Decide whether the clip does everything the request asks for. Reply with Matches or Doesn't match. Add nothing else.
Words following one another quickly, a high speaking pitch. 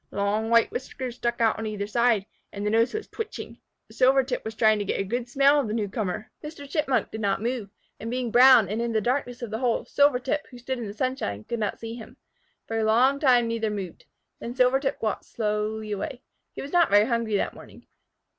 Matches